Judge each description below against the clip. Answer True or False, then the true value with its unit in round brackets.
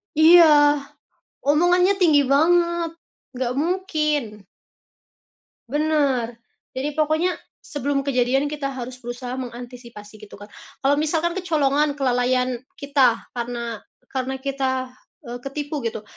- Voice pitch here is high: True (275 Hz)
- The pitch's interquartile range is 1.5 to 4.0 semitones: True (3.6 semitones)